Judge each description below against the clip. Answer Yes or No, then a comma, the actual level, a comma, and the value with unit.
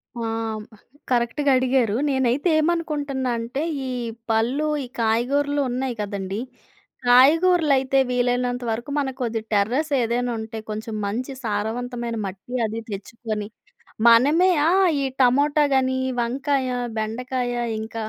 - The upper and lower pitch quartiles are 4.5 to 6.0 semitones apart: No, average, 3.2 semitones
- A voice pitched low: No, high, 245 Hz